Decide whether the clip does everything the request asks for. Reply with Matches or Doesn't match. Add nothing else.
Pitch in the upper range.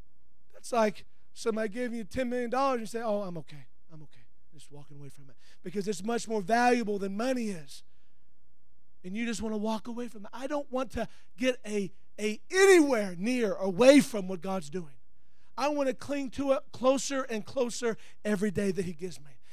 Matches